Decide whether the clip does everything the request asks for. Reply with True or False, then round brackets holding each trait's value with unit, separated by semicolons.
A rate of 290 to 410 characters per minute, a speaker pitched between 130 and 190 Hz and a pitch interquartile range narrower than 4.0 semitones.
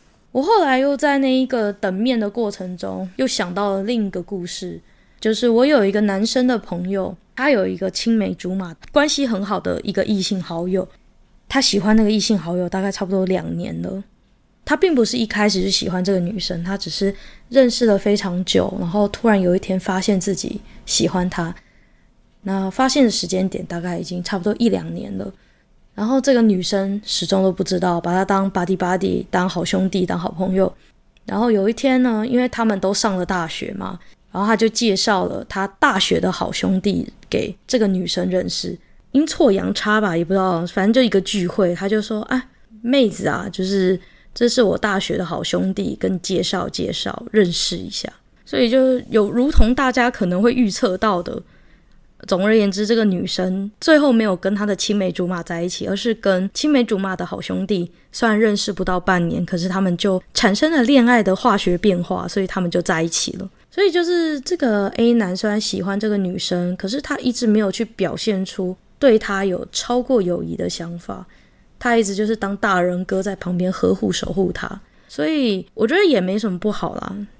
False (300 characters per minute; 200 Hz; 3.6 semitones)